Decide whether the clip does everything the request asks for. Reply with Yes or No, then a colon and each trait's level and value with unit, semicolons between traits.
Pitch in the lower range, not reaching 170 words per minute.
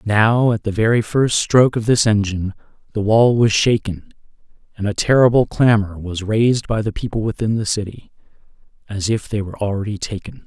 No: low, 110 Hz; average, 180 wpm